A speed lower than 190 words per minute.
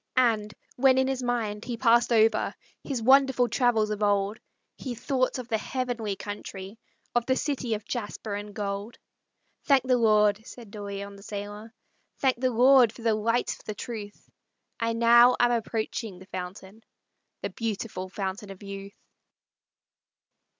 Yes: average, 155 wpm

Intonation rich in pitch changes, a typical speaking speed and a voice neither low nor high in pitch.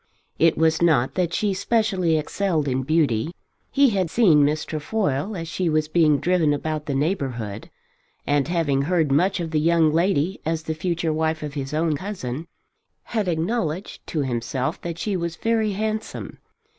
No: average, 3.6 semitones; average, 170 wpm; medium, 160 Hz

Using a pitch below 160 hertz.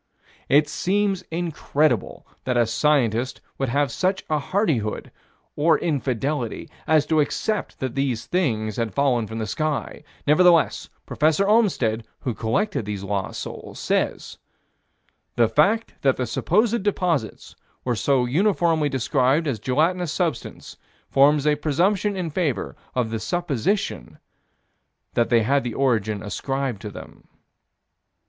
Yes: medium, 140 Hz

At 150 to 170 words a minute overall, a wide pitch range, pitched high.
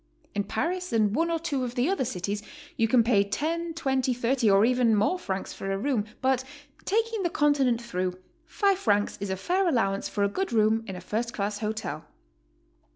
No: average, 200 wpm; wide, 6.5 semitones; high, 235 Hz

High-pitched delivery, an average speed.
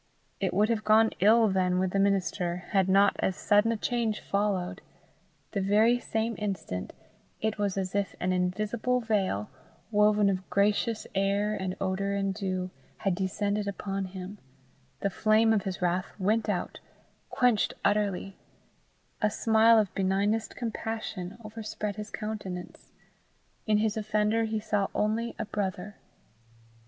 Yes: high, 205 Hz; average, 145 wpm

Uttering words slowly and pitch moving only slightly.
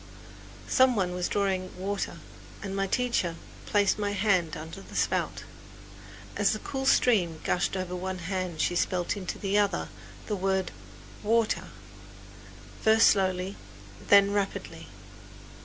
Yes: slow, 130 wpm; narrow, 2.0 semitones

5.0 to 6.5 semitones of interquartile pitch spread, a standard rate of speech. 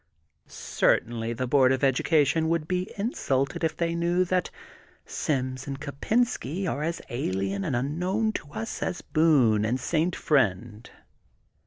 Yes: average, 5.3 semitones; average, 150 wpm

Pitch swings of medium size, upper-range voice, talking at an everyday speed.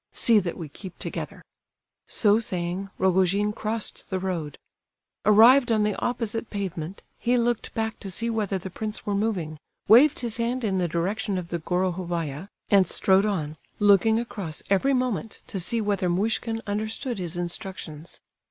Yes: average, 3.8 semitones; high, 200 Hz; average, 160 wpm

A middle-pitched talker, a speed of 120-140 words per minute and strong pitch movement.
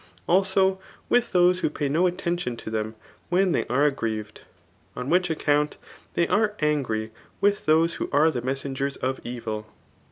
No: medium, 150 Hz; average, 160 wpm; wide, 6.2 semitones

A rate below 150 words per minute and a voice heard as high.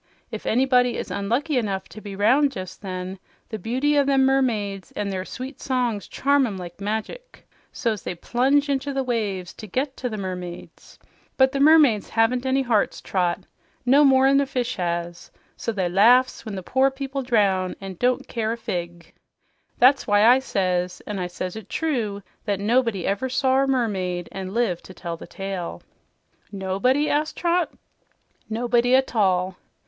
No: average, 175 wpm; high, 225 Hz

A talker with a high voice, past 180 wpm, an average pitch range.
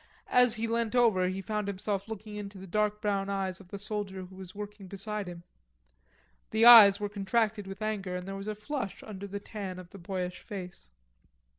No: high, 200 Hz; average, 200 wpm; narrow, 1.9 semitones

